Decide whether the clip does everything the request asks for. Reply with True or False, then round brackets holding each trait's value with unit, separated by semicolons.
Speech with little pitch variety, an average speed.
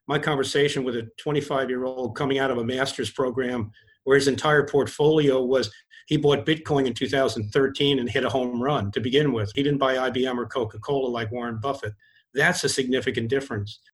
True (2.2 semitones; 195 wpm)